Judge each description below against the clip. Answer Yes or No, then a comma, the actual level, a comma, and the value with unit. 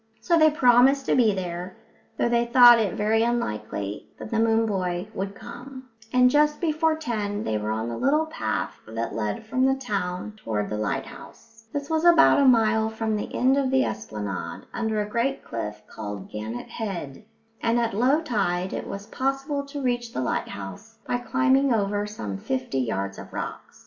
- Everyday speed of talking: Yes, average, 185 wpm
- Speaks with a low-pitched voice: No, high, 225 Hz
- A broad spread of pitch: Yes, wide, 6.9 semitones